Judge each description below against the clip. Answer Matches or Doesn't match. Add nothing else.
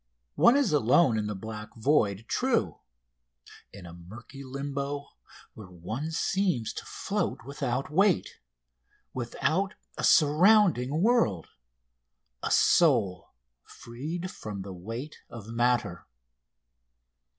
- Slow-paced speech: Matches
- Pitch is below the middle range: Matches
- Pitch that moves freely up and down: Matches